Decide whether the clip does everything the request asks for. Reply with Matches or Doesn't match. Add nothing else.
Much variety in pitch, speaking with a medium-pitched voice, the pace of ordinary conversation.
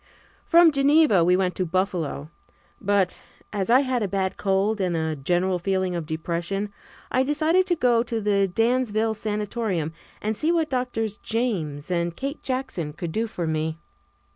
Doesn't match